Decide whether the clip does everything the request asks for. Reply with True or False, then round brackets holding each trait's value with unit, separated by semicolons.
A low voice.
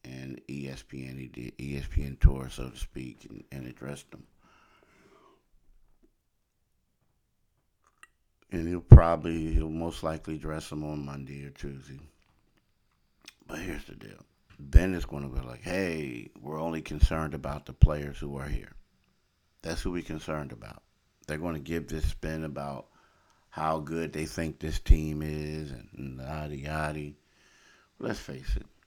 True (75 Hz)